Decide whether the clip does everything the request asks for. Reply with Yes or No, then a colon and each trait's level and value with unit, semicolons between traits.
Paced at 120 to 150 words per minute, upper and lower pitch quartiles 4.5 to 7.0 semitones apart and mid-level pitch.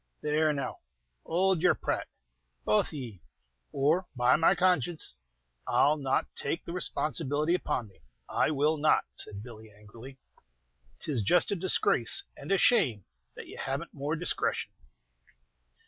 Yes: average, 145 wpm; wide, 5.4 semitones; medium, 150 Hz